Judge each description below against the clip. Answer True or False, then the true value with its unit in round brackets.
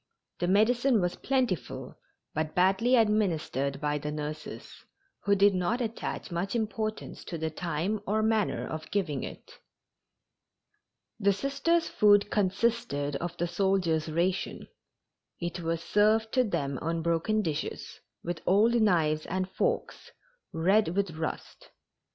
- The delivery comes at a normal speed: False (130 wpm)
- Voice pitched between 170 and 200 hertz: True (190 Hz)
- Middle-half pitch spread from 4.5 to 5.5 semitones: True (4.9 semitones)